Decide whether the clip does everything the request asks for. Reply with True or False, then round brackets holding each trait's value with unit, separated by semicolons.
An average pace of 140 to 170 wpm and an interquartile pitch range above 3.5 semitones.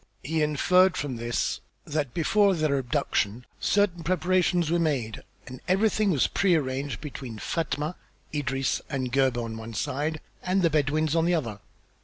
True (155 wpm; 4.9 semitones)